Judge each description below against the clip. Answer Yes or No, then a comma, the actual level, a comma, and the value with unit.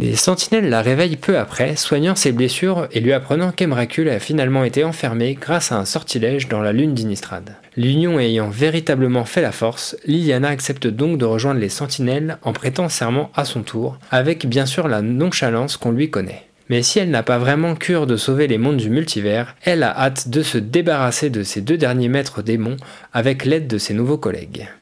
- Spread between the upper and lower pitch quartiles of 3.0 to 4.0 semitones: No, average, 4.8 semitones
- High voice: No, low, 135 Hz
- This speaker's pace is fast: No, average, 200 wpm